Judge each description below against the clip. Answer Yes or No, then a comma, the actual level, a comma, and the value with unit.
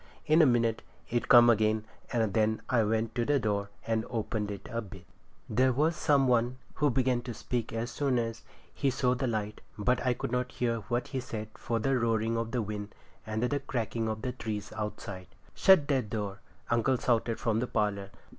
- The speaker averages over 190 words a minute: Yes, fast, 205 wpm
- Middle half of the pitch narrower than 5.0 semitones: Yes, narrow, 2.5 semitones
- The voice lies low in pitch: Yes, low, 115 Hz